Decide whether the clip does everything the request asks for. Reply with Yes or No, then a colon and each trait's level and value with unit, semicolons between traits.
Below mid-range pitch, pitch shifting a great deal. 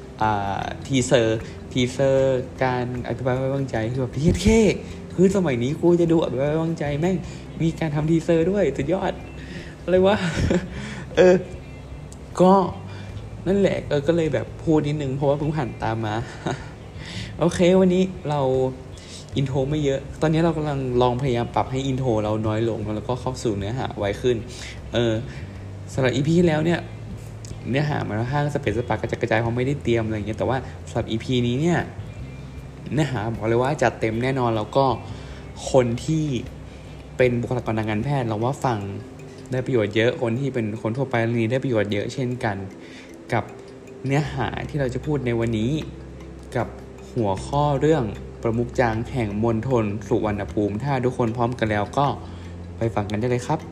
No: low, 125 Hz; average, 4.3 semitones